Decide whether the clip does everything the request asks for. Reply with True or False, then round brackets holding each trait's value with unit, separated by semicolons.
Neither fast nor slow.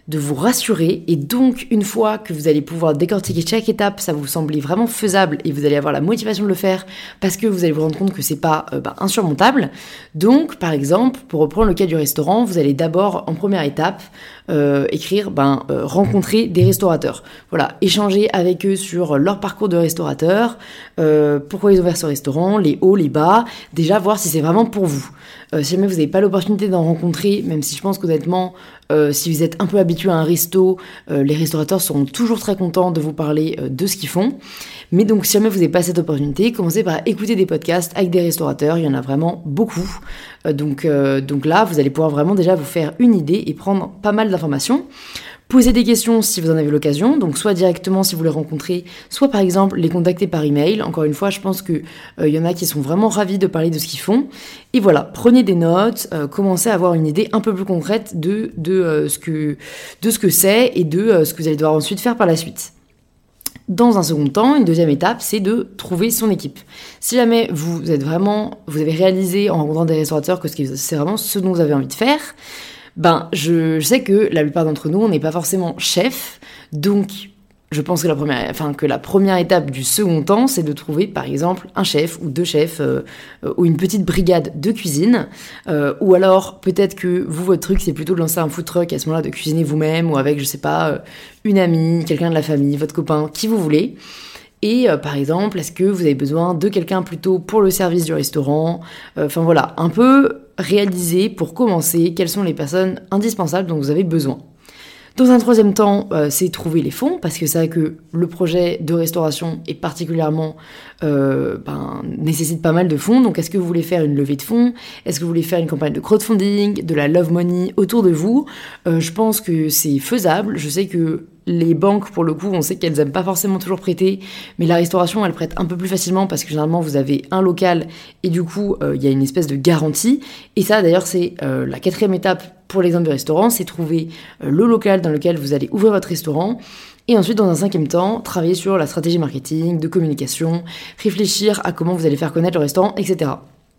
False (230 wpm)